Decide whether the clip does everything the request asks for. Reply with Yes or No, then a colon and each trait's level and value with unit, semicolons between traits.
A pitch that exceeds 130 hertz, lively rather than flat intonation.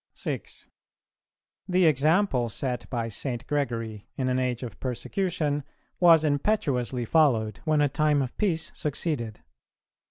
No: medium, 140 Hz; average, 4.4 semitones